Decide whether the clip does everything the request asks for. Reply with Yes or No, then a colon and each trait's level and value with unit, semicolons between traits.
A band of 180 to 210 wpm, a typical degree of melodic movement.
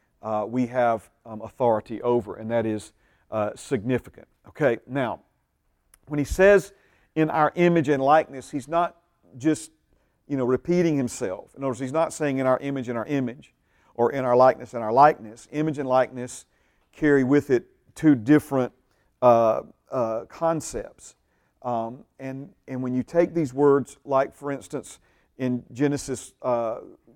No: average, 160 wpm; average, 4.0 semitones